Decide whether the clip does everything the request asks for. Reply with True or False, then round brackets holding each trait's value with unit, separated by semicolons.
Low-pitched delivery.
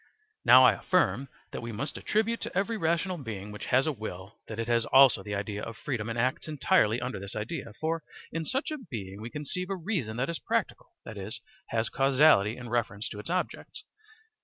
True (120 Hz)